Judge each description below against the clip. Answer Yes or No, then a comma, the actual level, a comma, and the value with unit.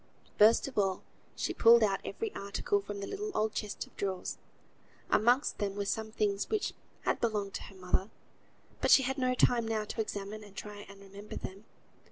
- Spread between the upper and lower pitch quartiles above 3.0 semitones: No, narrow, 2.6 semitones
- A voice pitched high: Yes, high, 210 Hz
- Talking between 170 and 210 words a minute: Yes, average, 195 wpm